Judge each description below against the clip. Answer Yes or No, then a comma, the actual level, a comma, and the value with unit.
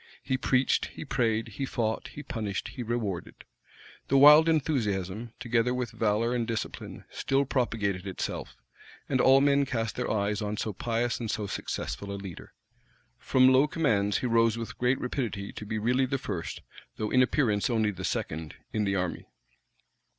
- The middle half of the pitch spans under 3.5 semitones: No, average, 3.9 semitones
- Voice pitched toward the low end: Yes, low, 115 Hz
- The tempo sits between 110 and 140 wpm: No, average, 170 wpm